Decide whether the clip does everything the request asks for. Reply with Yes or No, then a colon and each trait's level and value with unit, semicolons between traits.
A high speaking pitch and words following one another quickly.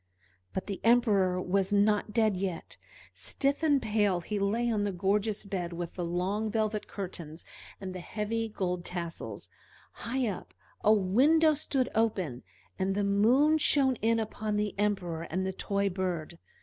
No: high, 205 Hz; average, 160 wpm